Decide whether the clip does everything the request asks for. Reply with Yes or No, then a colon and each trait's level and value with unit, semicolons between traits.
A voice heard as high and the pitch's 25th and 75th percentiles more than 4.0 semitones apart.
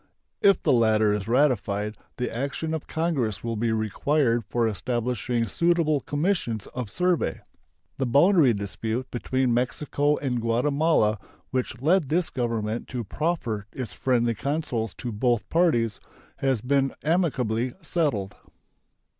No: low, 125 Hz; average, 4.7 semitones